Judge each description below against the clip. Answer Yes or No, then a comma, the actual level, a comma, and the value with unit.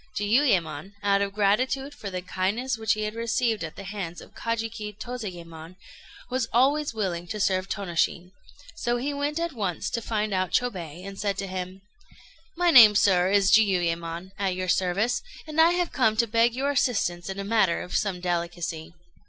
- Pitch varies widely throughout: No, average, 4.5 semitones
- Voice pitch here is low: No, high, 205 Hz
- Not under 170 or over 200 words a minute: Yes, average, 180 wpm